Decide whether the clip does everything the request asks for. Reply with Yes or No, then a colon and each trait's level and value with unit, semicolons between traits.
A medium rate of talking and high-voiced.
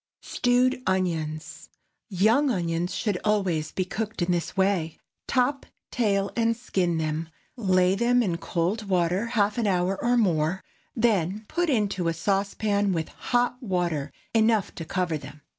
Yes: average, 150 wpm; high, 195 Hz